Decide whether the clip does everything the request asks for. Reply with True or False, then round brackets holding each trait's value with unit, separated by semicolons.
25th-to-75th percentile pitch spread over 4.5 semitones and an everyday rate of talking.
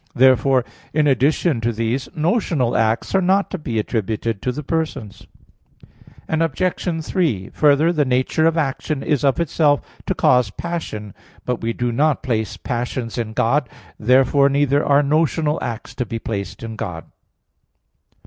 True (5.0 semitones; 150 wpm)